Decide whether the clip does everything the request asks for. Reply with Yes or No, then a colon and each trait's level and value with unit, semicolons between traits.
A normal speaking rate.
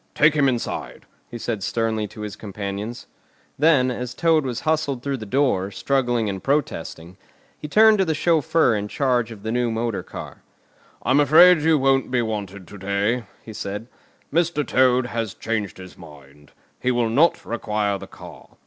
Yes: average, 175 wpm